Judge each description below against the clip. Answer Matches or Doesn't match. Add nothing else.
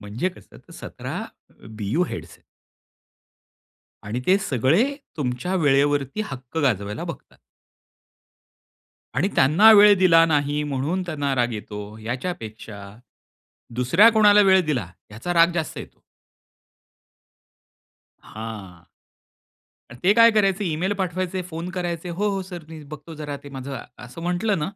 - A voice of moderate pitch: Matches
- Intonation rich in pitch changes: Matches